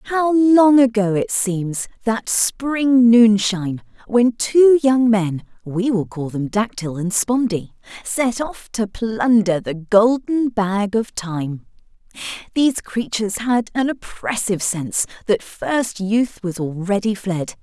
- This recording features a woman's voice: Yes, female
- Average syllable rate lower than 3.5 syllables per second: Yes, 3.3 syllables/s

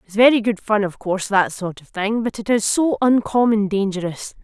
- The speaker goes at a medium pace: No, fast, 215 wpm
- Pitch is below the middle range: No, high, 210 Hz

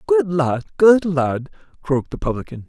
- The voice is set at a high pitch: No, medium, 145 Hz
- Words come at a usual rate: Yes, average, 155 wpm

